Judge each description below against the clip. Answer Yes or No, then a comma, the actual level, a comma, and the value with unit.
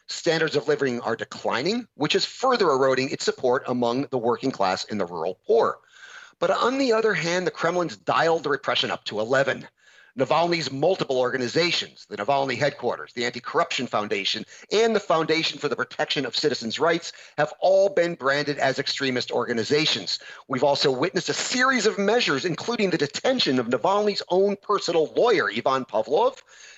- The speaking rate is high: No, average, 170 wpm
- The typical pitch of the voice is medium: Yes, medium, 165 Hz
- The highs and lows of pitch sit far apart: Yes, wide, 8.3 semitones